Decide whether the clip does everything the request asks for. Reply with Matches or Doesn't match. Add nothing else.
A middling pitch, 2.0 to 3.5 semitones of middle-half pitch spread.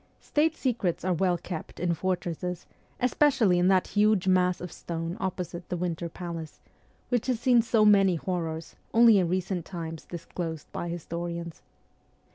Matches